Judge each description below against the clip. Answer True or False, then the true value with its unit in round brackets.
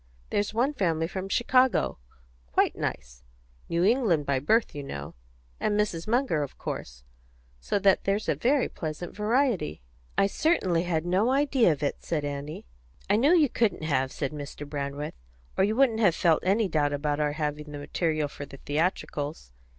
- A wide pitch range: True (6.7 semitones)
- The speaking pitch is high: False (170 Hz)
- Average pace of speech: True (175 wpm)